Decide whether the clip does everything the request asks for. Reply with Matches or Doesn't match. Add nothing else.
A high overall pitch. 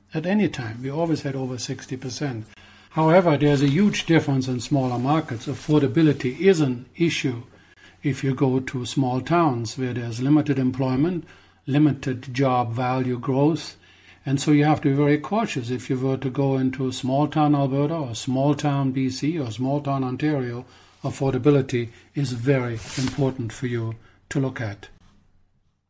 Doesn't match